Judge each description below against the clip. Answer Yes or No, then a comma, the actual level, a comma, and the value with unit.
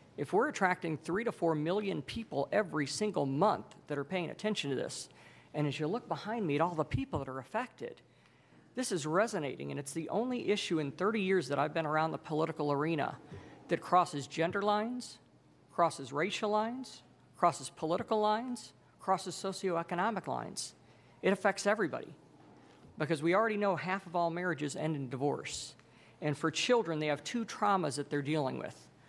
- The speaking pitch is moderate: Yes, medium, 165 Hz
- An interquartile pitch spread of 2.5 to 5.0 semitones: No, wide, 5.6 semitones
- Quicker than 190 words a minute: No, average, 175 wpm